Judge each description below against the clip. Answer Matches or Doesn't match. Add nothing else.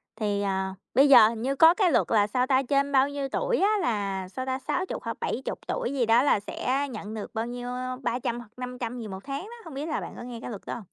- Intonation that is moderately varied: Matches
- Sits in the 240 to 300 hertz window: Matches